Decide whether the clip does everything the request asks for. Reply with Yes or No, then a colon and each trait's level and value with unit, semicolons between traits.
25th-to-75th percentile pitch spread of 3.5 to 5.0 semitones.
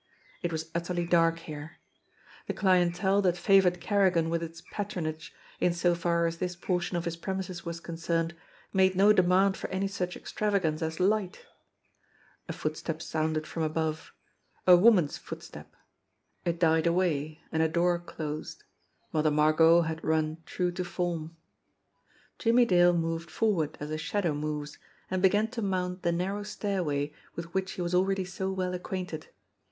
No: narrow, 2.6 semitones